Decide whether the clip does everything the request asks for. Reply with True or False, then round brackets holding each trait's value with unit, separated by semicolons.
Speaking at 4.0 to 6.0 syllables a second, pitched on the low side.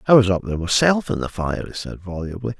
False (6.2 syllables/s; 100 Hz)